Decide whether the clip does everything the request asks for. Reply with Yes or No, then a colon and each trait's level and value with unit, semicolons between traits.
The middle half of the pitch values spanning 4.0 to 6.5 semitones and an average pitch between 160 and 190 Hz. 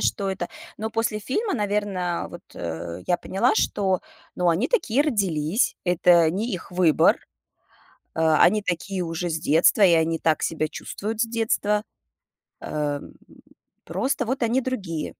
Yes: average, 5.0 semitones; medium, 185 Hz